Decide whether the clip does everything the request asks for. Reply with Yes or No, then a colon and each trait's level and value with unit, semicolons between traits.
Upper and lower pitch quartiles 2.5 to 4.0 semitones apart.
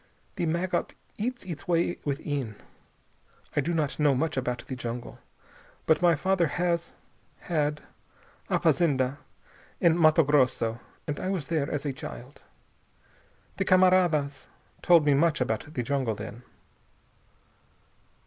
No: average, 4.4 semitones